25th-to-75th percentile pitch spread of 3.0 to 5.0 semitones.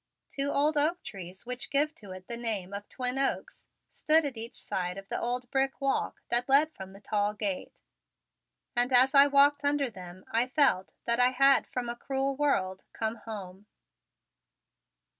No: wide, 5.4 semitones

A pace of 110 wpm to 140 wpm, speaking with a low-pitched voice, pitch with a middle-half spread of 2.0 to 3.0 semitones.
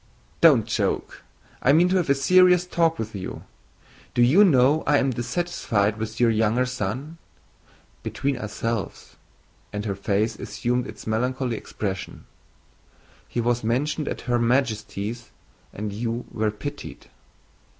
No: slow, 135 wpm; low, 120 Hz; average, 4.1 semitones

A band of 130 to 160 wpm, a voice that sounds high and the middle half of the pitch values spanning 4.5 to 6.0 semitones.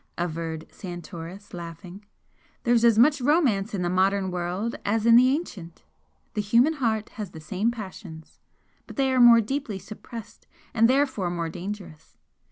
Yes: average, 155 wpm; high, 205 Hz; average, 5.1 semitones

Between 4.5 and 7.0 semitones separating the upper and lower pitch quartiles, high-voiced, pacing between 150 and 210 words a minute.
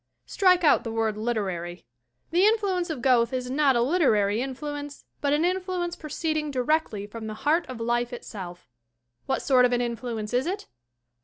Yes: wide, 5.6 semitones; very high, 255 Hz; average, 170 wpm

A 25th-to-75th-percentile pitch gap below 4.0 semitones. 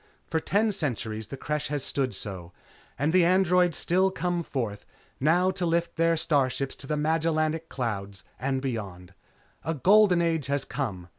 No: average, 5.1 semitones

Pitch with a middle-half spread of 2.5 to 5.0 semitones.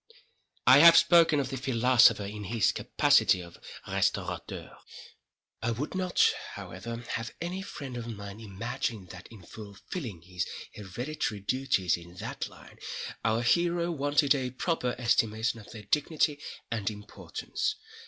No: wide, 5.6 semitones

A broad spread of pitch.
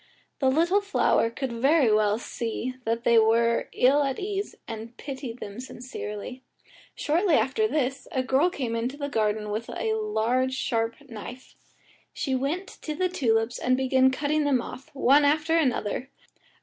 No: average, 4.3 semitones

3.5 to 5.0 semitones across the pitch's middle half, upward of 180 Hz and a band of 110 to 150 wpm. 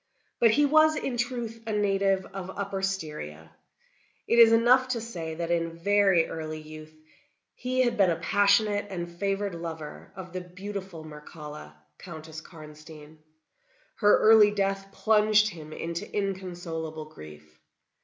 Yes: average, 4.6 semitones; high, 190 Hz; average, 140 wpm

